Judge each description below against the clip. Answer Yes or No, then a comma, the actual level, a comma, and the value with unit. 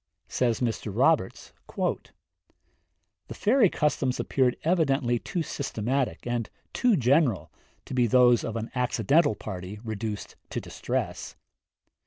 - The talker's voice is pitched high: No, low, 125 Hz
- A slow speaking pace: Yes, slow, 115 wpm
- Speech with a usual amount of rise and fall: Yes, average, 4.0 semitones